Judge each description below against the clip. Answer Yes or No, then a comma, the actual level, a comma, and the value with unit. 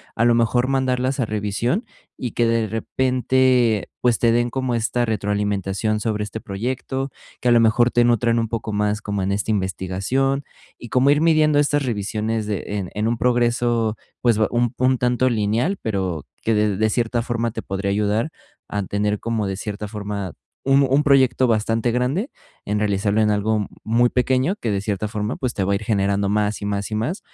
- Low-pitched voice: Yes, low, 115 Hz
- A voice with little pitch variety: No, average, 3.1 semitones